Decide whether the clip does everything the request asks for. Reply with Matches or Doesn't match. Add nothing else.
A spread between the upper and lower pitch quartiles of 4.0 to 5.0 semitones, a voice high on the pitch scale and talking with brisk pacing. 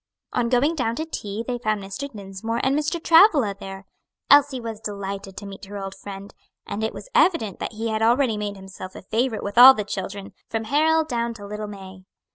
Matches